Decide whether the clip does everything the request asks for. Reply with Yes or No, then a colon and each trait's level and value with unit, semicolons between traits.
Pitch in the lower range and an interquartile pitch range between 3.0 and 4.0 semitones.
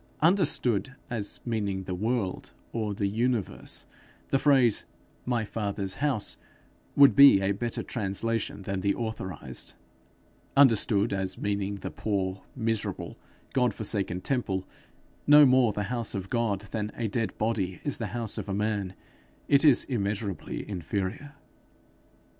Yes: low, 110 Hz; average, 3.6 semitones